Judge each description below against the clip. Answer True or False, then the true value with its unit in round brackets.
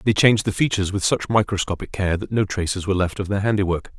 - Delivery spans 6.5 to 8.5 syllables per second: True (6.8 syllables/s)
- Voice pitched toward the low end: True (100 Hz)